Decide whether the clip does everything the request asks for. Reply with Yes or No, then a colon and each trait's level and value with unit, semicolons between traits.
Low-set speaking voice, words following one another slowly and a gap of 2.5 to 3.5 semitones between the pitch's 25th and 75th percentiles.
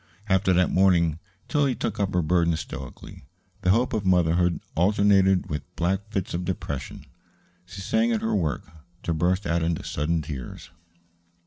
No: very low, 90 Hz; average, 155 wpm; average, 2.8 semitones